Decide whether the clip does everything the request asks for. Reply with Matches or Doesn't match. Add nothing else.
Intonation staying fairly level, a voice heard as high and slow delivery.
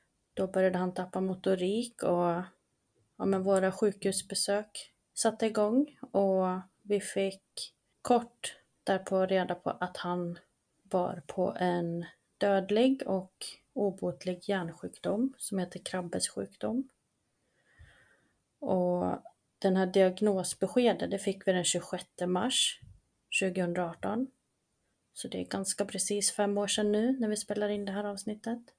Matches